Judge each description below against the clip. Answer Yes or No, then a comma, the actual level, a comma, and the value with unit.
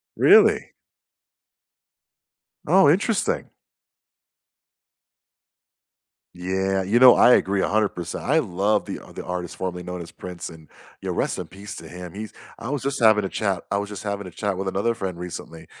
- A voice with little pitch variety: No, average, 3.3 semitones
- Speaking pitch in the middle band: No, very low, 95 Hz